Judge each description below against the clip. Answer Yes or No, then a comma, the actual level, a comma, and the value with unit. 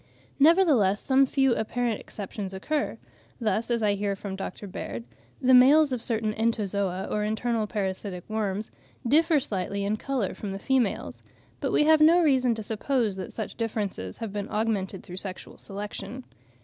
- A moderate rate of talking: Yes, average, 160 wpm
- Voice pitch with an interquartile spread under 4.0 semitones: No, average, 4.3 semitones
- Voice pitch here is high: Yes, high, 215 Hz